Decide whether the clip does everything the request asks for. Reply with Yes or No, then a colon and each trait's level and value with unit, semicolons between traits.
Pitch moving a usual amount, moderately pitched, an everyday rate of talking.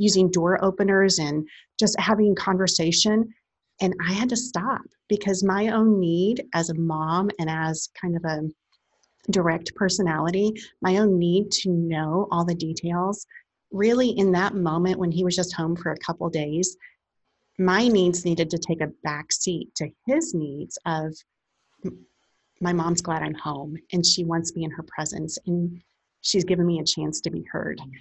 Yes: average, 3.0 semitones; medium, 175 Hz; average, 175 wpm